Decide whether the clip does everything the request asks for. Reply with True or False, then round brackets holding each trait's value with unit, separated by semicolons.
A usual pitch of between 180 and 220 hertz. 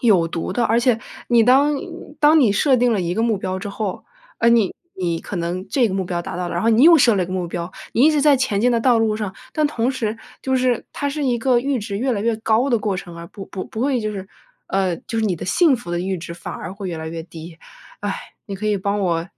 True (215 Hz)